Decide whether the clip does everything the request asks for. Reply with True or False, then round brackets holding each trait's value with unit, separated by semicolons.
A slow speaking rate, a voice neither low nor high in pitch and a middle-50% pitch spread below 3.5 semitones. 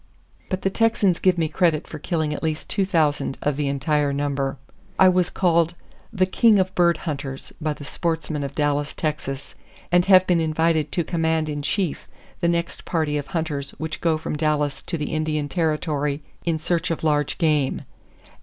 False (180 wpm; 155 Hz; 2.7 semitones)